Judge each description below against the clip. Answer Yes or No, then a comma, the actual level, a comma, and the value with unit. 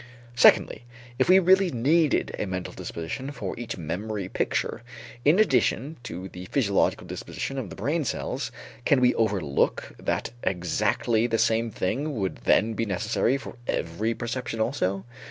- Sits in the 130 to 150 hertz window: No, low, 115 Hz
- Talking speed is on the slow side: No, average, 150 wpm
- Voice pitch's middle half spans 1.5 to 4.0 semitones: No, wide, 5.5 semitones